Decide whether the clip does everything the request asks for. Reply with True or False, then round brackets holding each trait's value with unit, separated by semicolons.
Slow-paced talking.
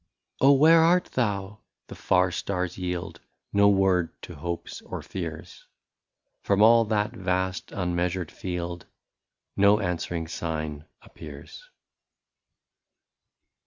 True (115 wpm)